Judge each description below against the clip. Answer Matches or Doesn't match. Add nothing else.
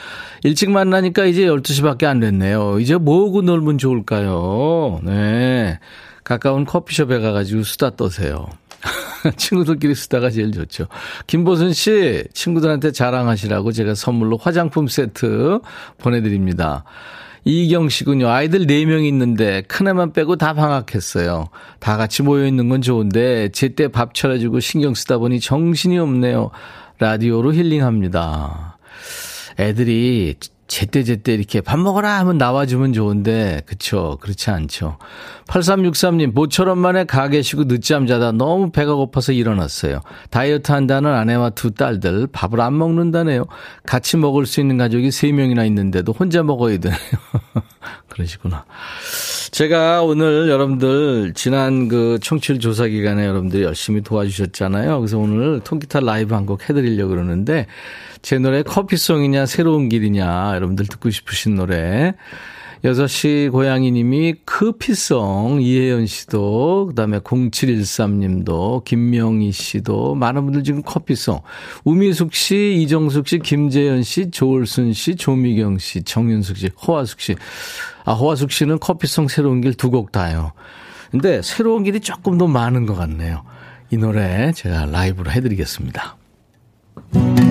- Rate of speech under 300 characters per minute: Doesn't match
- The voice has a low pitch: Matches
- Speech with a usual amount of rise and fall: Doesn't match